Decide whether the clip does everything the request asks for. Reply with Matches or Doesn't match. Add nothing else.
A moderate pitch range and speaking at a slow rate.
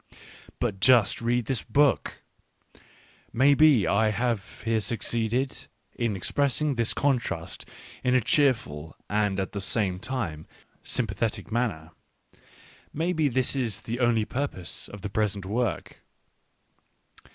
Matches